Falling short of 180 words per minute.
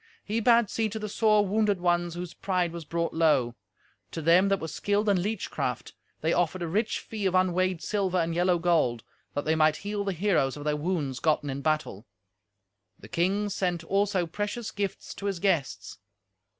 No: average, 190 wpm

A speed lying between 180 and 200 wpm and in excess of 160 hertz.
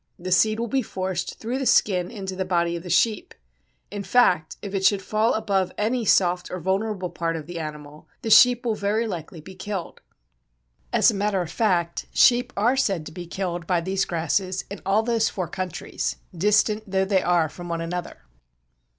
Yes: average, 195 wpm; high, 190 Hz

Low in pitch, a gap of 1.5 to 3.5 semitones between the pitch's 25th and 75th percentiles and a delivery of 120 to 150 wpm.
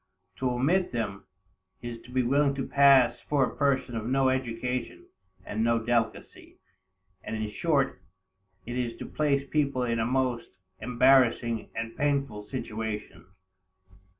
Yes: low, 125 Hz; average, 2.9 semitones; average, 140 wpm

